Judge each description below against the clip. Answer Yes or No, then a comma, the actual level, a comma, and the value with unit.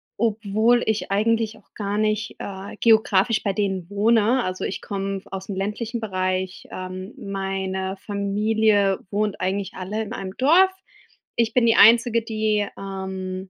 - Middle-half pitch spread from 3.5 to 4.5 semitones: No, narrow, 2.4 semitones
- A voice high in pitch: Yes, high, 205 Hz